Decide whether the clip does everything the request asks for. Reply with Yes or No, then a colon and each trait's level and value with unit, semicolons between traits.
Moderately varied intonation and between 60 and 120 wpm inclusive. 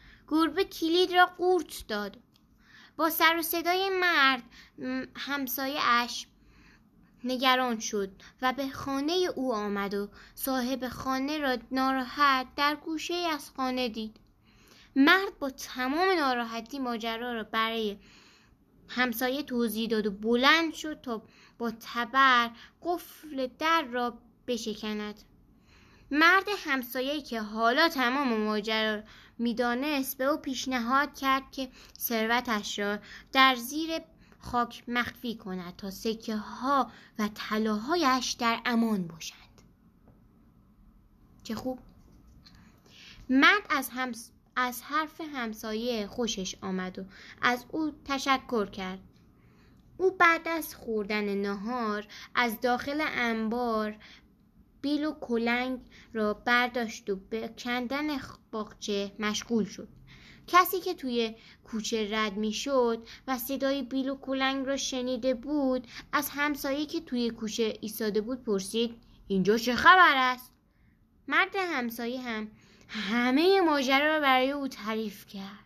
Yes: average, 4.0 semitones; average, 115 wpm